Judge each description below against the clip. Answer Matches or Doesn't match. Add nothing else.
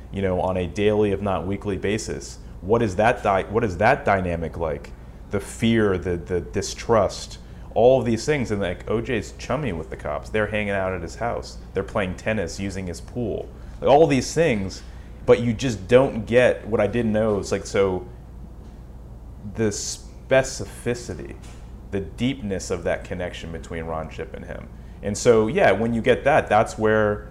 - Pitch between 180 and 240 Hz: Doesn't match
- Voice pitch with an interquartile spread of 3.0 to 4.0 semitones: Matches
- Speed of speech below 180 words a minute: Doesn't match